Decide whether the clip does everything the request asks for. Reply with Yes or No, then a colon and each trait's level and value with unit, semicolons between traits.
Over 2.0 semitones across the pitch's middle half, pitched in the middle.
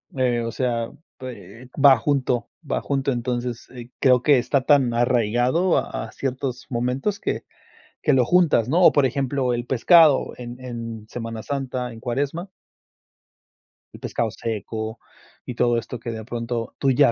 No: narrow, 2.4 semitones; low, 125 Hz